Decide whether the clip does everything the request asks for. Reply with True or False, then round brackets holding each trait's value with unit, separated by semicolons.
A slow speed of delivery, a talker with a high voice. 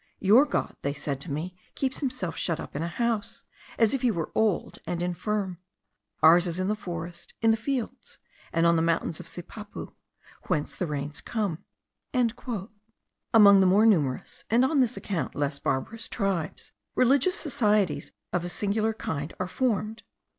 False (170 wpm; 195 Hz)